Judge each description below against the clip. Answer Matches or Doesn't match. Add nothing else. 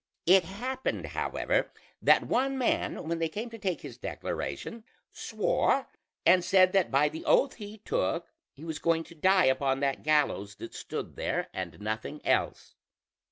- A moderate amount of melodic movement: Doesn't match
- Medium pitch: Matches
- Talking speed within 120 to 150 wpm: Doesn't match